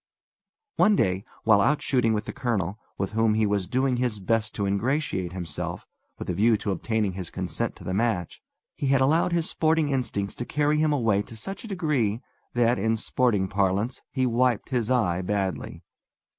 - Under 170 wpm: No, average, 185 wpm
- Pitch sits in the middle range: No, low, 115 Hz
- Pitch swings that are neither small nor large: Yes, average, 4.7 semitones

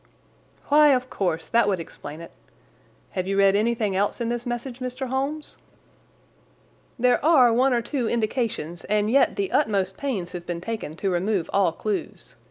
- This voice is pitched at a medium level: No, high, 225 Hz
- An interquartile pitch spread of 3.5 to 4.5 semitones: No, average, 4.9 semitones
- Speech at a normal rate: Yes, average, 170 wpm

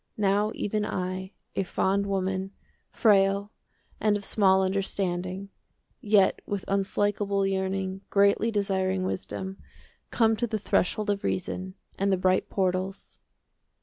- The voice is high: Yes, high, 195 Hz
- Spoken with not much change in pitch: Yes, narrow, 1.3 semitones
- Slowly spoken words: Yes, slow, 125 wpm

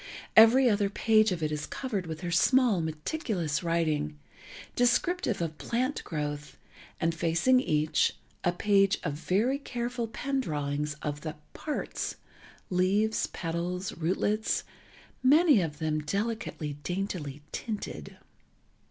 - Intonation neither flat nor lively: No, wide, 6.7 semitones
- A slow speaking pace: Yes, slow, 115 wpm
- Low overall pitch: No, medium, 180 Hz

